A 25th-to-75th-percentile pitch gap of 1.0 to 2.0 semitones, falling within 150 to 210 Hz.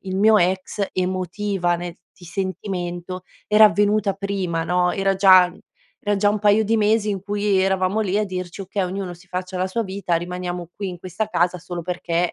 No: narrow, 2.4 semitones; medium, 185 Hz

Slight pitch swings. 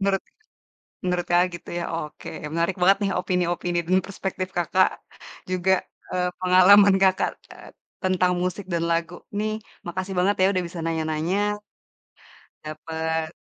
Yes: narrow, 2.0 semitones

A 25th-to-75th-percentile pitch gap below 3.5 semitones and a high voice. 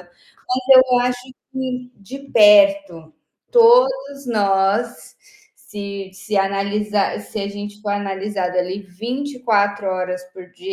No: average, 4.6 semitones; high, 205 Hz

